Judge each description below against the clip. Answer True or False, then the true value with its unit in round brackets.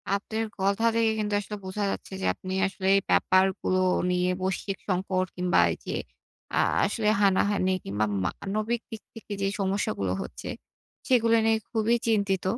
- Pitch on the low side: False (200 Hz)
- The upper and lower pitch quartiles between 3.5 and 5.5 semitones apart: False (2.6 semitones)